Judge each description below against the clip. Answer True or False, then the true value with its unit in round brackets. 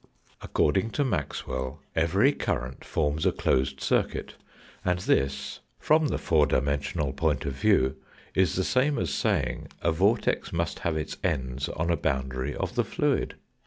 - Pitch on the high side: False (80 Hz)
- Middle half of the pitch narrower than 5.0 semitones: False (5.4 semitones)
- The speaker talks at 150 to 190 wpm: True (155 wpm)